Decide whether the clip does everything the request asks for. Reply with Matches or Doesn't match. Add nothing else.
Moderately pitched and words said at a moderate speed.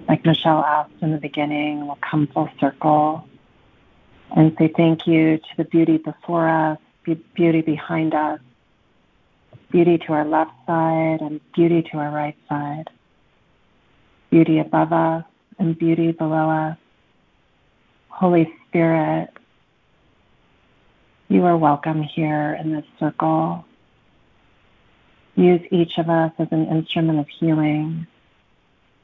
Doesn't match